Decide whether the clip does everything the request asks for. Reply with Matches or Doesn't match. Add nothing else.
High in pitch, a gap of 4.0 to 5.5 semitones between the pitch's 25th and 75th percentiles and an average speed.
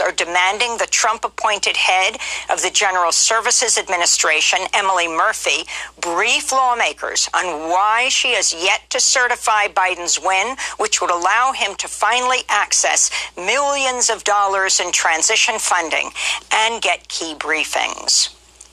Doesn't match